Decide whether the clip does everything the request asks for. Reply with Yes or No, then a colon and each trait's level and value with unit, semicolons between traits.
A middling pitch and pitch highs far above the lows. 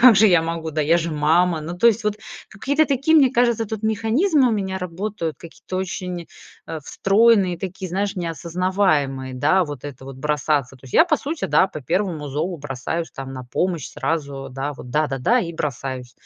Yes: medium, 170 Hz; wide, 5.7 semitones